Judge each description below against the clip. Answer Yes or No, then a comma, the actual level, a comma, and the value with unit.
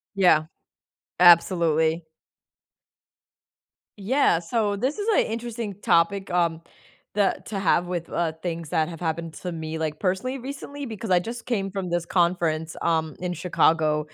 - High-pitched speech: No, medium, 175 Hz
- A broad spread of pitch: No, average, 3.7 semitones